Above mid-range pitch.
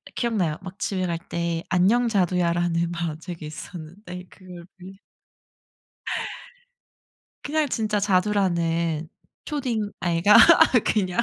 No: medium, 180 Hz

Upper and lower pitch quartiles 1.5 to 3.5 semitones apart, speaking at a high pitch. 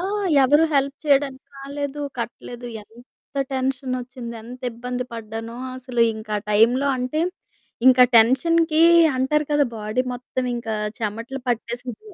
Yes: average, 2.8 semitones; very high, 250 Hz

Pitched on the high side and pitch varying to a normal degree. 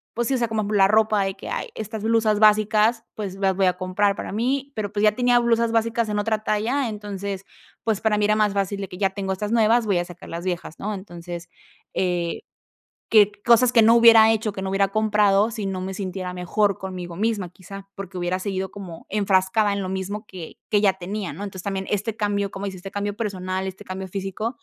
No: high, 200 Hz; narrow, 2.3 semitones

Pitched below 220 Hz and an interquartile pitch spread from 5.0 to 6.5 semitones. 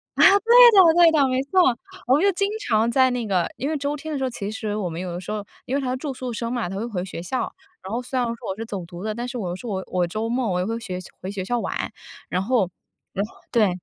No: high, 235 Hz; wide, 5.5 semitones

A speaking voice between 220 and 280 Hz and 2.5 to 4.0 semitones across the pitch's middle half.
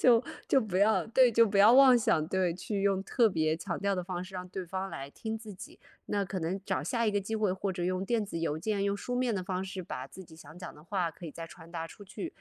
No: high, 190 Hz; average, 3.6 semitones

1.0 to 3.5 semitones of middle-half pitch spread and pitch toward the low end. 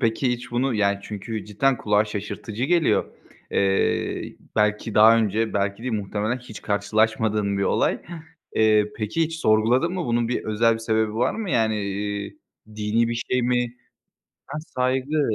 Yes: average, 2.7 semitones; low, 110 Hz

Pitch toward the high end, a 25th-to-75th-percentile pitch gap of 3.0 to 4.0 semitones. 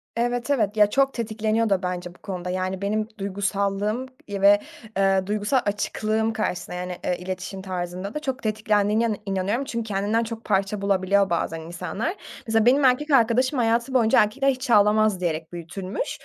Yes: high, 210 Hz; average, 3.3 semitones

